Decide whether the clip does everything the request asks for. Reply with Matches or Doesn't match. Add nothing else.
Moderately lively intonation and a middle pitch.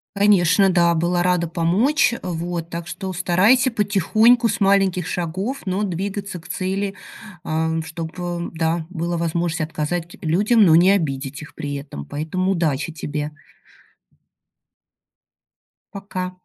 Matches